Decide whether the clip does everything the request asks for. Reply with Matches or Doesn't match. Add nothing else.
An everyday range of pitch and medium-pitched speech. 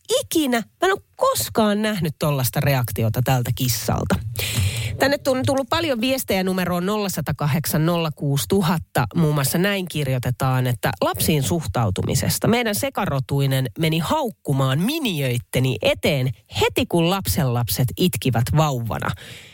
Doesn't match